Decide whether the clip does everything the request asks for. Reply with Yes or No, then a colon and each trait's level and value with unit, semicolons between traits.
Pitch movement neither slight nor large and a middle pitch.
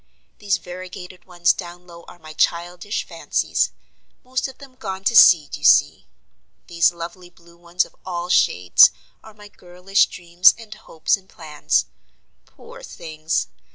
No: narrow, 2.2 semitones; medium, 175 Hz